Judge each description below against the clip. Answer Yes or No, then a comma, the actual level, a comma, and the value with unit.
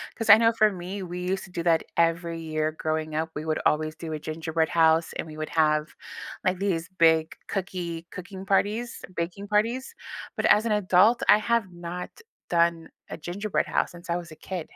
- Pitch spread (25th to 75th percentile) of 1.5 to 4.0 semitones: Yes, average, 3.4 semitones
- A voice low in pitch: No, medium, 175 Hz